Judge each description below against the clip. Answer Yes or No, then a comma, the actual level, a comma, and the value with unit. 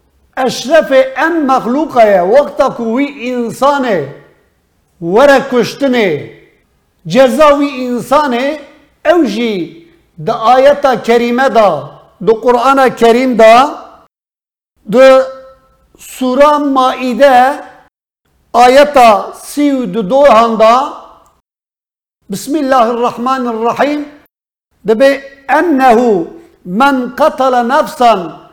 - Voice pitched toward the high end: Yes, very high, 260 Hz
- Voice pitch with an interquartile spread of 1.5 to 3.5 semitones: Yes, average, 3.2 semitones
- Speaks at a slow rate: Yes, slow, 75 wpm